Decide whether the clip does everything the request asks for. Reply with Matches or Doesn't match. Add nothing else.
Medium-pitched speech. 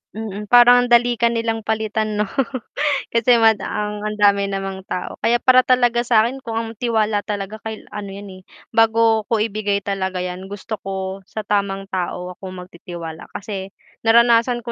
Doesn't match